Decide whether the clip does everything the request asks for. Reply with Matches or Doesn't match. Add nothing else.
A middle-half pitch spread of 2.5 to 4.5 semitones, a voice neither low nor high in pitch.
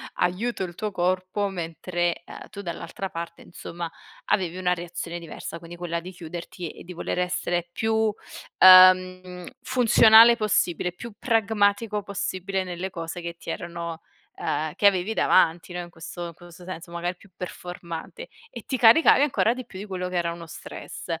Matches